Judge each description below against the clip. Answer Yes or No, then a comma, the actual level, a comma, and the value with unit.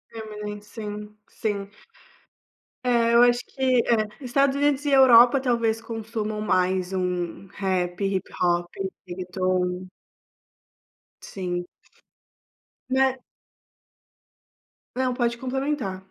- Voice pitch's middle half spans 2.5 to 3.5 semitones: No, average, 4.9 semitones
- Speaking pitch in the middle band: No, high, 215 Hz